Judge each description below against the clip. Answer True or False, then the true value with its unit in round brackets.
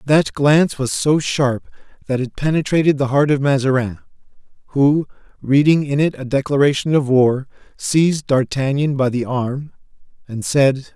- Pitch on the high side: False (140 Hz)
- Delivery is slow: False (150 wpm)